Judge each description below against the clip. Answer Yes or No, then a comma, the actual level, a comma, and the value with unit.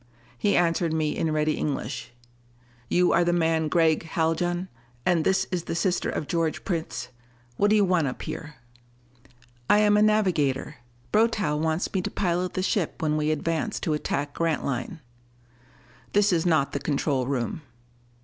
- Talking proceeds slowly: No, average, 160 wpm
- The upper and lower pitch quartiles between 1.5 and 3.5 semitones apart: Yes, average, 3.0 semitones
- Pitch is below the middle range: No, medium, 165 Hz